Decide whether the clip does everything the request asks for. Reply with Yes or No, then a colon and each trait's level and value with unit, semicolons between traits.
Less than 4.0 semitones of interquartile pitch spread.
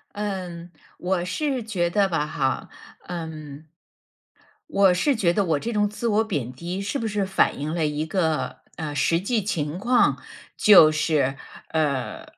No: average, 4.9 semitones